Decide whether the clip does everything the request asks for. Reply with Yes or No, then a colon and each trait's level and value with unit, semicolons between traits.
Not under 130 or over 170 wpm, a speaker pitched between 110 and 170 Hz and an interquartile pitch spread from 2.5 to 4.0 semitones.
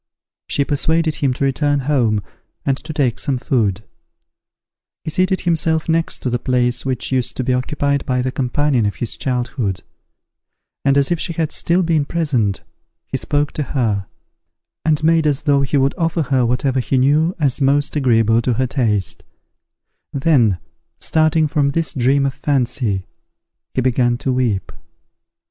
Yes: average, 160 wpm; low, 135 Hz; average, 3.3 semitones